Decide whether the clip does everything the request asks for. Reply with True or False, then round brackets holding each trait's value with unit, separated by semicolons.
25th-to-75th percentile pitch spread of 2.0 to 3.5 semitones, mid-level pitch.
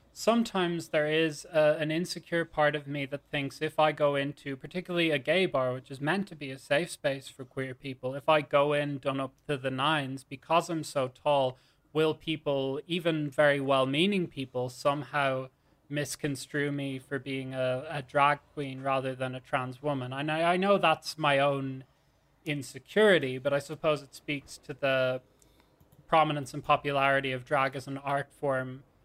True (2.4 semitones; 145 Hz)